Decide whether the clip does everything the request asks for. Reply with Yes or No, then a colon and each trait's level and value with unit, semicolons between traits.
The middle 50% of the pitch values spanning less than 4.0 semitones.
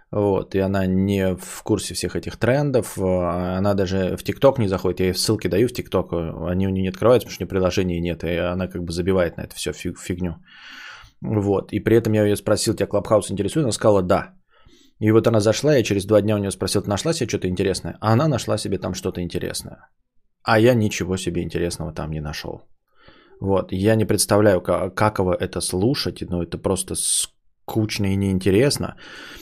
Yes: average, 3.0 semitones